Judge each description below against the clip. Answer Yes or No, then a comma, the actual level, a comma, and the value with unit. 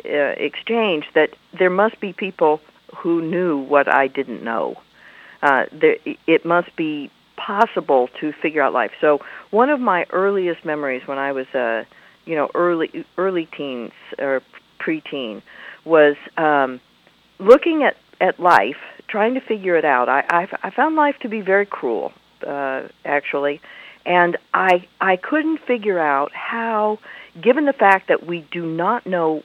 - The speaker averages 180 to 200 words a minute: No, average, 155 wpm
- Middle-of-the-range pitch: Yes, medium, 175 Hz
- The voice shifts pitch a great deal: Yes, wide, 7.0 semitones